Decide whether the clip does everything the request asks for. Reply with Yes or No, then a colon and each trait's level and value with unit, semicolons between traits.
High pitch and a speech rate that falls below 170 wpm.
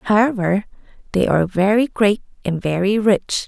Yes: high, 200 Hz; average, 140 wpm